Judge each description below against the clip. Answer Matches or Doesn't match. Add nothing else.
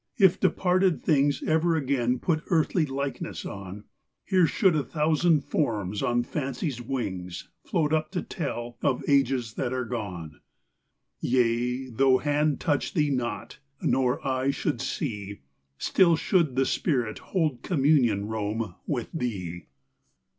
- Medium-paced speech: Doesn't match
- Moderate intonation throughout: Matches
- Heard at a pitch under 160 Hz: Matches